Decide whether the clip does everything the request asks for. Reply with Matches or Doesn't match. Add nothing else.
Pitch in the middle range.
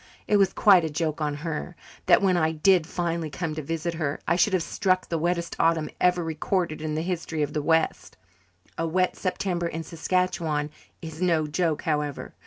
Matches